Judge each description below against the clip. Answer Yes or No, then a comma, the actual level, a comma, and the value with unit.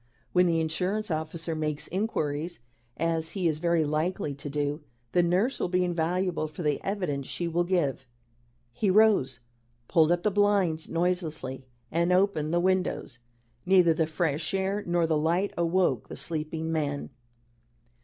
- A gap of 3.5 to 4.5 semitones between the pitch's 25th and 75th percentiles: No, average, 2.8 semitones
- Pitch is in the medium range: Yes, medium, 170 Hz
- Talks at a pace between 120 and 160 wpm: Yes, average, 155 wpm